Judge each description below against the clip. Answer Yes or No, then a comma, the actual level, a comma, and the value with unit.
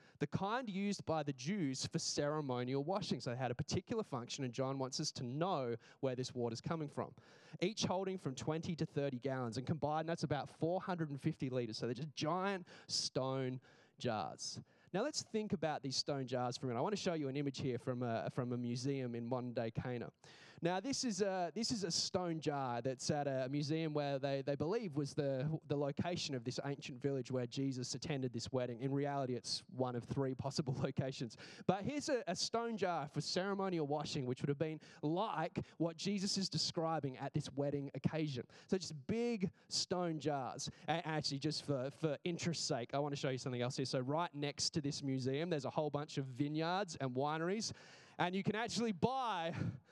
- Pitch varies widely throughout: No, average, 4.4 semitones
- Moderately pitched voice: Yes, medium, 150 Hz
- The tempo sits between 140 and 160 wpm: No, fast, 205 wpm